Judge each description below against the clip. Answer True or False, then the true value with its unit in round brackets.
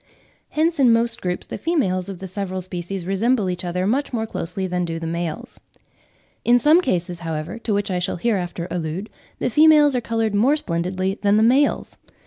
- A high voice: True (195 Hz)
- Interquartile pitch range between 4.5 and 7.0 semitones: True (5.1 semitones)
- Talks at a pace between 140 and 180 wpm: False (190 wpm)